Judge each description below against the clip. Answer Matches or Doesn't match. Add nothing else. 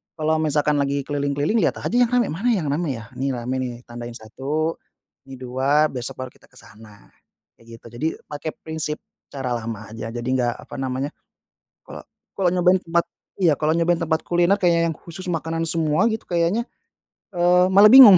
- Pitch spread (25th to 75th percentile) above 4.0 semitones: Matches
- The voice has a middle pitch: Matches